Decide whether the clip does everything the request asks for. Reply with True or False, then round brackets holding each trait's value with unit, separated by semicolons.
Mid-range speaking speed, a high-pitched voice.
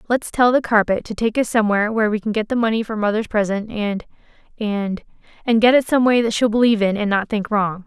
False (230 wpm; 220 Hz)